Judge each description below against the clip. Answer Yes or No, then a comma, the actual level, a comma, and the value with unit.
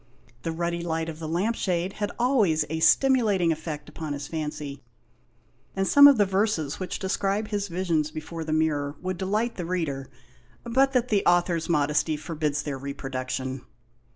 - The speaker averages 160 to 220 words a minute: Yes, average, 165 wpm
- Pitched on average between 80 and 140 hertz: No, medium, 170 Hz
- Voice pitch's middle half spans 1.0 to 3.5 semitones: No, average, 4.5 semitones